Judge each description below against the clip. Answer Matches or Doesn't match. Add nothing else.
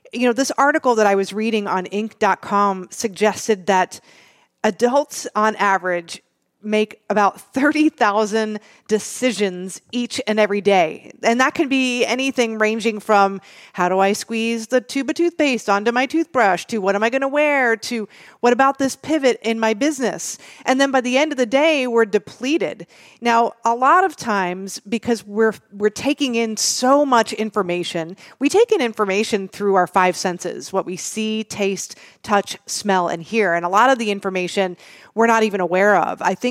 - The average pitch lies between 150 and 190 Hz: Doesn't match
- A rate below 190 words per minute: Matches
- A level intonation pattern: Doesn't match